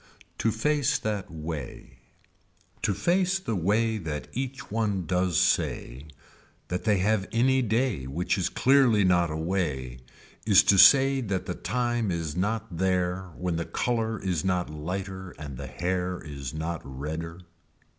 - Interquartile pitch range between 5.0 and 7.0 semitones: Yes, average, 5.3 semitones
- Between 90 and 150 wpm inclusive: Yes, average, 145 wpm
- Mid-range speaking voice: No, very low, 95 Hz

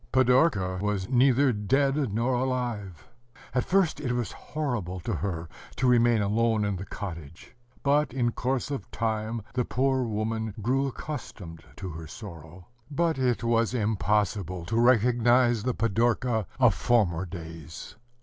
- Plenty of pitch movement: No, average, 4.5 semitones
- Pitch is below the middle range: Yes, low, 115 Hz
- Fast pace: No, average, 140 wpm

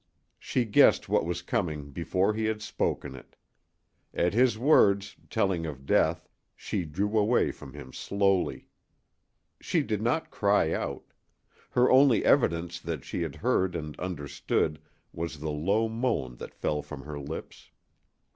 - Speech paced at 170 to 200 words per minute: No, average, 145 wpm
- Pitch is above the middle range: No, very low, 90 Hz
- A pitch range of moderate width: No, wide, 5.8 semitones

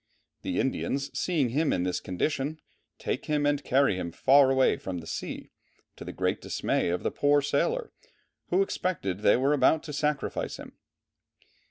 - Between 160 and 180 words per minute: Yes, average, 170 wpm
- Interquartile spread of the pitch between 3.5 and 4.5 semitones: Yes, average, 3.9 semitones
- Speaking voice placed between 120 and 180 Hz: Yes, medium, 140 Hz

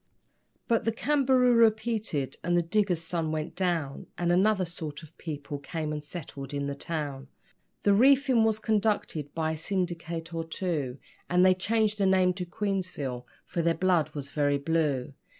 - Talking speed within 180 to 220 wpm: No, average, 170 wpm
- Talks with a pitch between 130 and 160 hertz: No, medium, 170 Hz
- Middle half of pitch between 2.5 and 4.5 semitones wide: No, average, 5.1 semitones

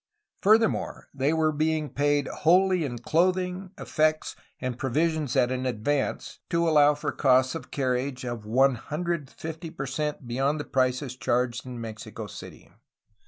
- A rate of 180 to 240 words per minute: No, average, 145 wpm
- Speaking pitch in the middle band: Yes, medium, 145 Hz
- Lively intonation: No, average, 3.9 semitones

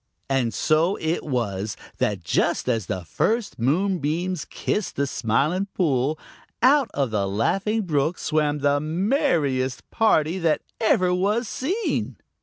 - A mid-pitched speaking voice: Yes, medium, 155 Hz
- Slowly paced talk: Yes, slow, 130 wpm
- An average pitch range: No, wide, 6.9 semitones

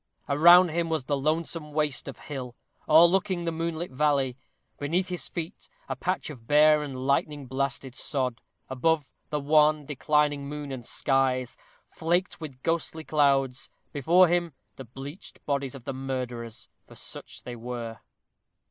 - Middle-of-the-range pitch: Yes, medium, 145 Hz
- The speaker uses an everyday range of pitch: Yes, average, 3.4 semitones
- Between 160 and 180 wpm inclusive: No, average, 150 wpm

